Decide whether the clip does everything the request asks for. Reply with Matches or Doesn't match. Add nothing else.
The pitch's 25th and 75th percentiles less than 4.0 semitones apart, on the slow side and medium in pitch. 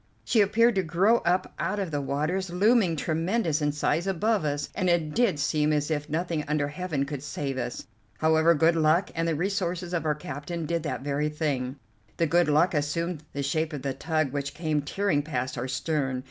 Doesn't match